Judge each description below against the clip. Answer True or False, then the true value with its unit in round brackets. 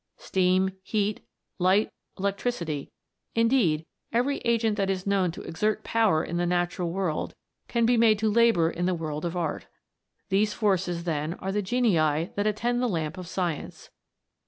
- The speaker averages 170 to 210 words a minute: False (160 wpm)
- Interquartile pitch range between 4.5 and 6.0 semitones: False (4.1 semitones)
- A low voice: False (190 Hz)